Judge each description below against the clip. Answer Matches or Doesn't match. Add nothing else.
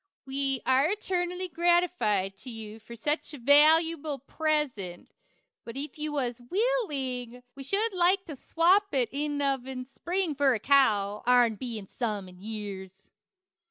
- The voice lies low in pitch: Doesn't match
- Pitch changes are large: Matches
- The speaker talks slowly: Doesn't match